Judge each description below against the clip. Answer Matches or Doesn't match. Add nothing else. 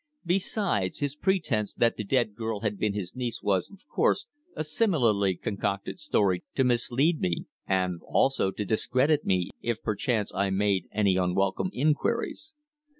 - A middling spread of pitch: Doesn't match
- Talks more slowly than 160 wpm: Matches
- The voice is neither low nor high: Doesn't match